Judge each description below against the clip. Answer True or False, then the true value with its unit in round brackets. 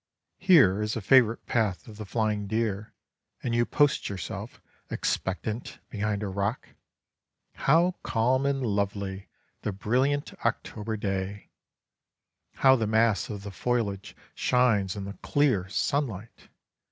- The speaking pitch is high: False (110 Hz)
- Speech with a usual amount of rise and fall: True (3.6 semitones)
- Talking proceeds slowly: True (130 wpm)